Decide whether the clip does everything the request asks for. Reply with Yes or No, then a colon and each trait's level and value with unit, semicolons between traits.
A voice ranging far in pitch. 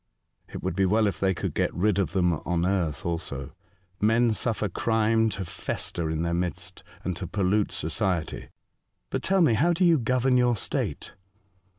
No: average, 4.6 semitones